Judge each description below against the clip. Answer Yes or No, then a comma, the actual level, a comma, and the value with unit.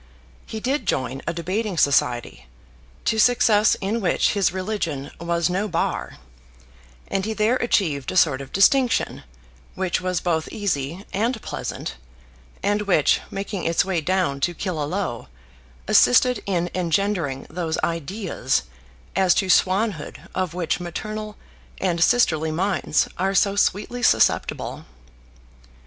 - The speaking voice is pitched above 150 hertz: Yes, medium, 185 Hz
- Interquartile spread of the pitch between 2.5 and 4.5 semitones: Yes, average, 4.1 semitones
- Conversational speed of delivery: No, slow, 130 wpm